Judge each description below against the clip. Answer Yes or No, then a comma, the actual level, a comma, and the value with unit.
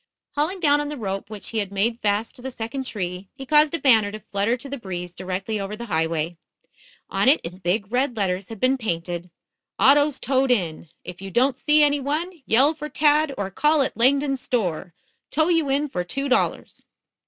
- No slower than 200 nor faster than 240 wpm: Yes, fast, 205 wpm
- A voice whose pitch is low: No, high, 235 Hz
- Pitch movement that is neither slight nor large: No, wide, 6.5 semitones